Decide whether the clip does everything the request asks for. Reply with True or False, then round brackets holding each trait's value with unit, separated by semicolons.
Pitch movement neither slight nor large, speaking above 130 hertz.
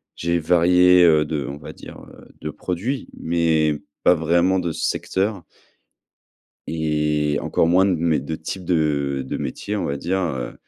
False (3.0 semitones; 80 Hz)